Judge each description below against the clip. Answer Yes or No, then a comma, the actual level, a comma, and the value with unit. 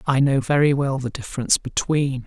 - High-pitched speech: No, low, 135 Hz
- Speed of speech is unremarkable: Yes, average, 185 wpm